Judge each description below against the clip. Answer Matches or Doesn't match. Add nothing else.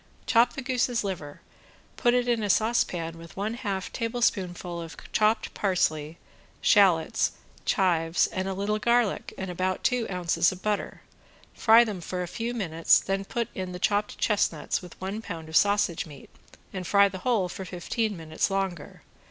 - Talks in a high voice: Matches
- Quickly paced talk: Doesn't match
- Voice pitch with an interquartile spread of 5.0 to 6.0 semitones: Doesn't match